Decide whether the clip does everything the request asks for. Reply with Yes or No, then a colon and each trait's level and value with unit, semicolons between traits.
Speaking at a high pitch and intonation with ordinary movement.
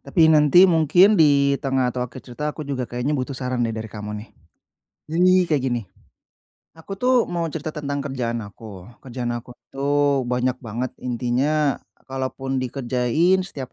No: low, 135 Hz; average, 3.6 semitones